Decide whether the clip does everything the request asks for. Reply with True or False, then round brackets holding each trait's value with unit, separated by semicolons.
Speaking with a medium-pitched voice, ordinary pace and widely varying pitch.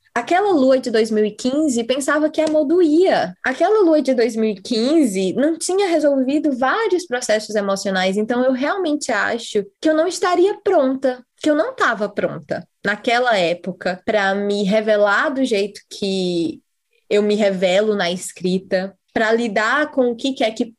False (245 Hz; 145 wpm; 6.7 semitones)